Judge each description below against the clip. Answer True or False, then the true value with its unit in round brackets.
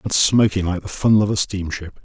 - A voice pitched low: True (95 Hz)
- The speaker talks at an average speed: False (235 wpm)